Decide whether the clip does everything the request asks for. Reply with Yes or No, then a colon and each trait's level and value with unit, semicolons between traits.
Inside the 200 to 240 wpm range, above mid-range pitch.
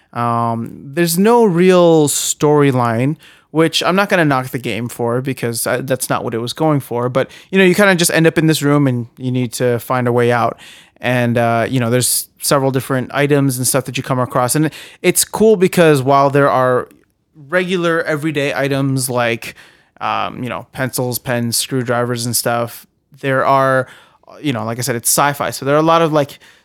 No: fast, 205 wpm; low, 135 Hz